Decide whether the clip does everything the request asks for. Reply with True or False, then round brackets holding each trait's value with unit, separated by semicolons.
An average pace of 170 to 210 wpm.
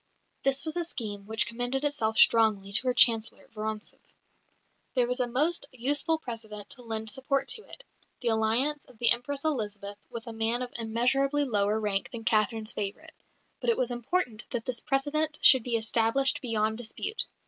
True (175 wpm)